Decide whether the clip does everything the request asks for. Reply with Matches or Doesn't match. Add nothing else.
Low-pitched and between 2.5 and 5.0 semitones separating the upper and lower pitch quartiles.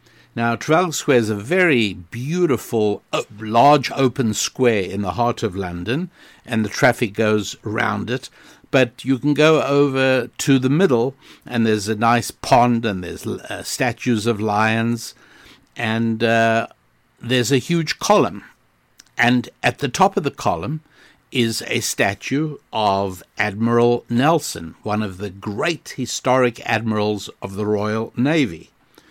Matches